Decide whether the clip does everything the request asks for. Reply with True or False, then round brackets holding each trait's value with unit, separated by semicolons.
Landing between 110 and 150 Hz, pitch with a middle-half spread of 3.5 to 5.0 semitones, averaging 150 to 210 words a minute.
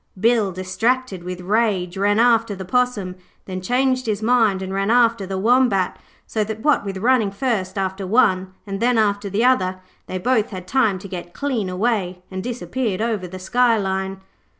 False (205 Hz; 4.0 semitones; 175 wpm)